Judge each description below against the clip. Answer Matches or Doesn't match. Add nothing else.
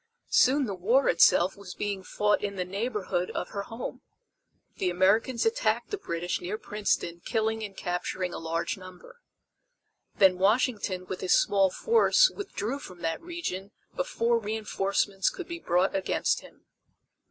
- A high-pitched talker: Matches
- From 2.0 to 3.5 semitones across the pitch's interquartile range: Doesn't match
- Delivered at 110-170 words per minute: Matches